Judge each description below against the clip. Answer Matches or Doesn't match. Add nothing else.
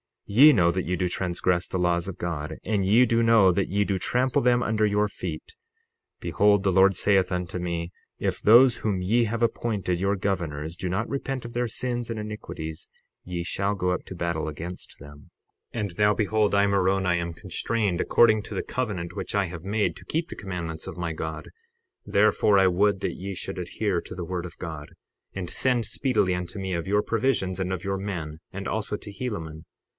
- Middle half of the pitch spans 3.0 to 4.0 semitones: Matches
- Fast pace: Matches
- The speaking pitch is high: Doesn't match